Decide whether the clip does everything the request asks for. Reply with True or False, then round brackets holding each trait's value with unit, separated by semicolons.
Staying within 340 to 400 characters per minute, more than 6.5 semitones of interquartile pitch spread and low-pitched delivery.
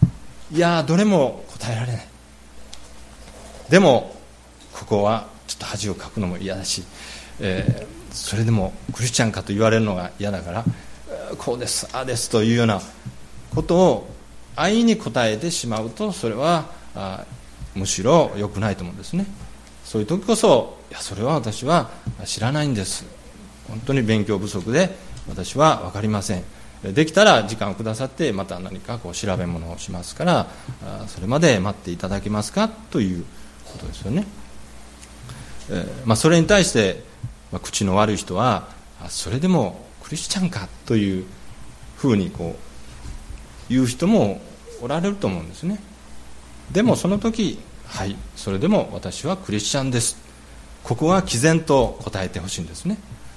False (305 characters per minute; 8.1 semitones; 110 Hz)